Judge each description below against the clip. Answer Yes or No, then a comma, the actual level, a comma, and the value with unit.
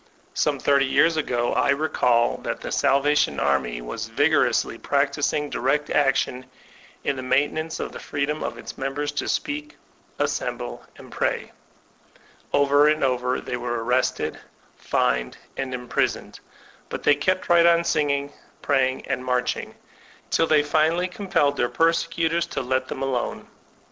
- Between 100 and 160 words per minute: Yes, average, 145 wpm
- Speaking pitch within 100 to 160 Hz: Yes, medium, 140 Hz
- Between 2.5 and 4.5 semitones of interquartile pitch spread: Yes, average, 3.4 semitones